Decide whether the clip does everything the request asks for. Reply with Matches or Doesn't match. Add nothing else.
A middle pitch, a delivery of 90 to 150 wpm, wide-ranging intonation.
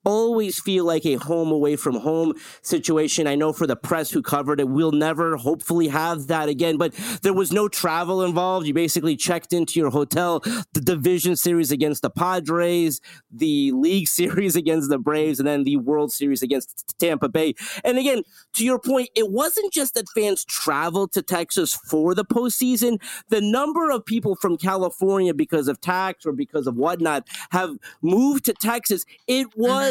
Doesn't match